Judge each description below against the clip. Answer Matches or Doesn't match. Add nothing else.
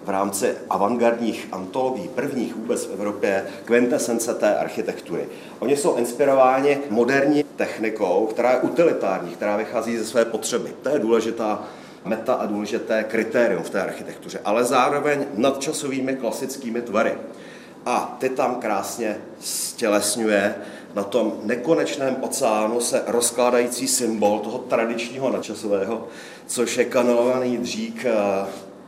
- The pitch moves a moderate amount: Matches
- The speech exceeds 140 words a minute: Doesn't match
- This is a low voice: Matches